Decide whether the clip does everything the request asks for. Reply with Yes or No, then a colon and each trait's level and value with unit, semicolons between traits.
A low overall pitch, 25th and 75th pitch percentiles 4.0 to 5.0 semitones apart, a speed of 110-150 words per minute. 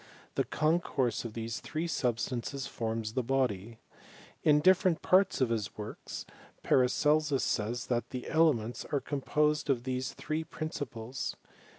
Yes: low, 130 Hz; average, 4.6 semitones; average, 140 wpm